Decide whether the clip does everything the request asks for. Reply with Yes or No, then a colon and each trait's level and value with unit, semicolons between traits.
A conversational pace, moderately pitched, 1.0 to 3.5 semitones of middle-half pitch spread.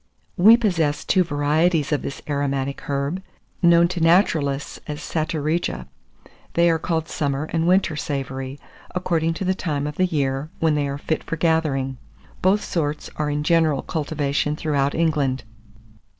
Yes: average, 150 wpm; medium, 155 Hz; average, 2.9 semitones